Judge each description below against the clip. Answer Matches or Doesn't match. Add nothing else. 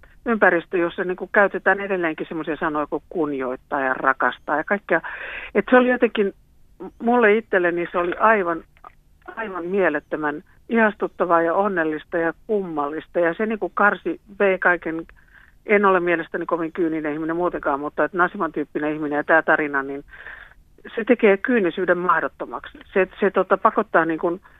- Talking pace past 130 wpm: Matches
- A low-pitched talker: Doesn't match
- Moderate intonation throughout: Matches